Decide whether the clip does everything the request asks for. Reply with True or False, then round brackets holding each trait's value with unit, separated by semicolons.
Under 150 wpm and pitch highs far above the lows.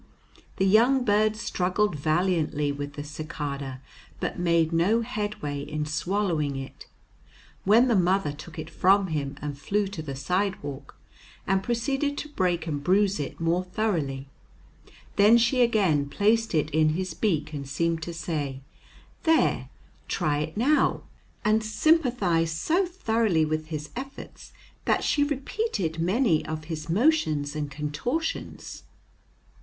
True (140 wpm; 6.1 semitones)